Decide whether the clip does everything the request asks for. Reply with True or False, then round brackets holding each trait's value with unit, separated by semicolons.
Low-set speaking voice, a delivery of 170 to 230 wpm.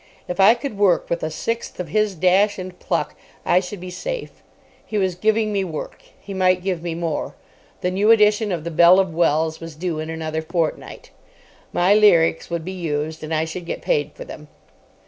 False (180 Hz; 205 wpm)